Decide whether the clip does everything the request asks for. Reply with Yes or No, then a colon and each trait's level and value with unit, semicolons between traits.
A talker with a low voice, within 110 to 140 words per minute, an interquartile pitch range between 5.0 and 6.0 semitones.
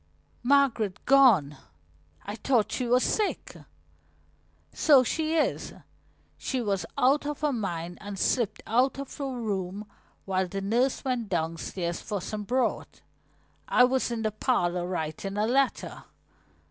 No: high, 225 Hz; slow, 135 wpm; wide, 5.5 semitones